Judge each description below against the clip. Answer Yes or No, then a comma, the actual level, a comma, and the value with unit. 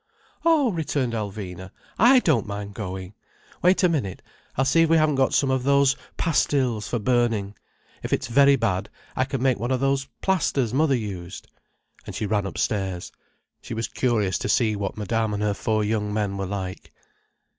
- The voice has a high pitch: No, low, 115 Hz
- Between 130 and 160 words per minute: No, average, 180 wpm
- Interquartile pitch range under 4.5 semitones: No, average, 5.2 semitones